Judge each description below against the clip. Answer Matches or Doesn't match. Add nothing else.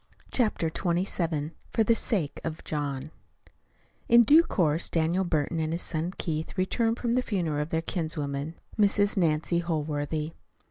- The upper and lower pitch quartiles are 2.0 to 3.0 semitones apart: Doesn't match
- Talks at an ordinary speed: Matches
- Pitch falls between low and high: Matches